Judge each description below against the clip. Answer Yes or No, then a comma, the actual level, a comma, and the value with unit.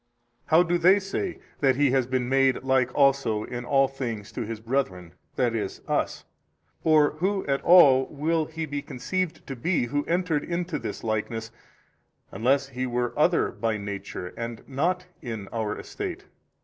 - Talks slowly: No, average, 170 wpm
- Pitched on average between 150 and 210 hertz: No, low, 135 Hz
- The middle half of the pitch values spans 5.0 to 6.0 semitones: Yes, wide, 5.4 semitones